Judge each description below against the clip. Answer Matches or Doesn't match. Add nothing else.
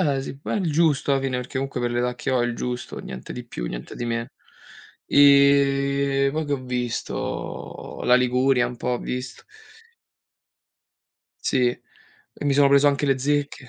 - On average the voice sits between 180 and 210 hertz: Doesn't match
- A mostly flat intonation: Matches